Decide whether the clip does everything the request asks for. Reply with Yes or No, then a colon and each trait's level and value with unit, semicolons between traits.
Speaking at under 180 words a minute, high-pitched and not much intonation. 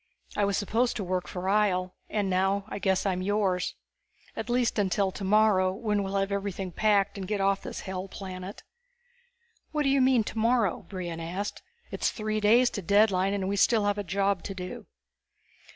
No: average, 185 wpm; high, 200 Hz; narrow, 2.1 semitones